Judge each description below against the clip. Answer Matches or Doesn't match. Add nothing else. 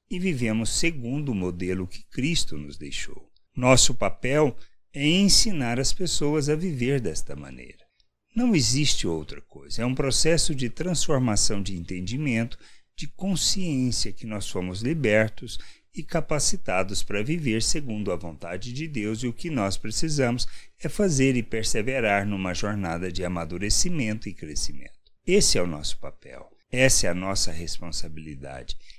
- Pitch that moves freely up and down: Matches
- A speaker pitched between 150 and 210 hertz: Doesn't match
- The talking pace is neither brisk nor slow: Matches